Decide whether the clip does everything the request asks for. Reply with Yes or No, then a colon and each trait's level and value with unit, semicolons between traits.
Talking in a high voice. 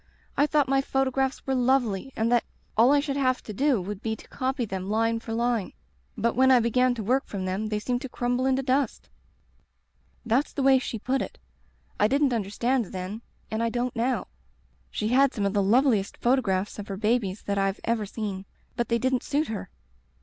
Yes: high, 235 Hz